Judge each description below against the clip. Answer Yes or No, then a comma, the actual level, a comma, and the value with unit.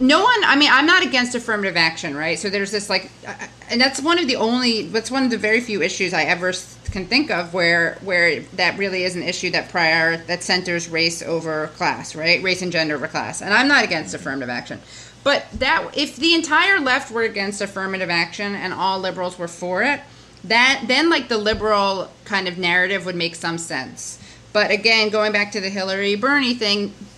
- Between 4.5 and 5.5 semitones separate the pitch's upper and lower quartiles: Yes, average, 5.1 semitones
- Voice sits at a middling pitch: No, high, 195 Hz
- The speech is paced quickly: Yes, fast, 210 wpm